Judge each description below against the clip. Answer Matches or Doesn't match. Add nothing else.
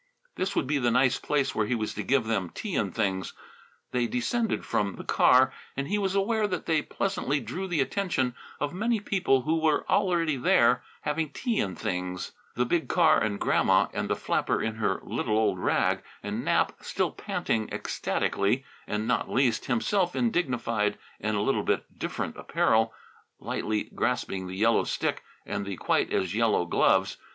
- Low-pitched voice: Matches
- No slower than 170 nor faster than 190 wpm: Matches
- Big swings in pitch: Matches